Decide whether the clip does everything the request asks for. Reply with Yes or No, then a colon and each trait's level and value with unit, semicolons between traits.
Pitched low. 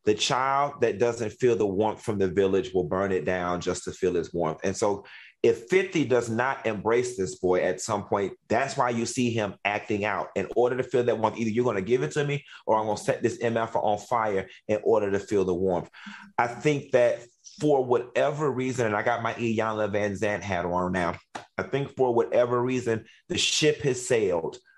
Yes: low, 115 Hz